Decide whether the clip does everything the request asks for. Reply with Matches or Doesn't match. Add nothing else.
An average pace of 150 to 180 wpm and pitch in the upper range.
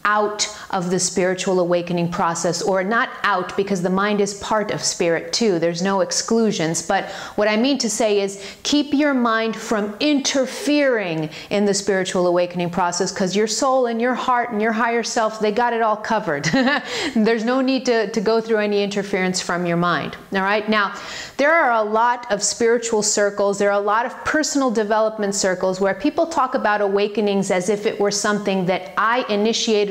Doesn't match